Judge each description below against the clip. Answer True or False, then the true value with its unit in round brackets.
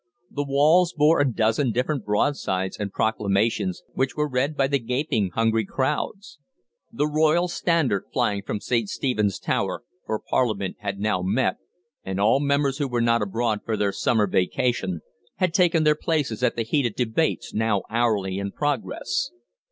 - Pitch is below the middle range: True (120 Hz)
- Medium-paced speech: True (165 wpm)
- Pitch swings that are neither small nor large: False (5.9 semitones)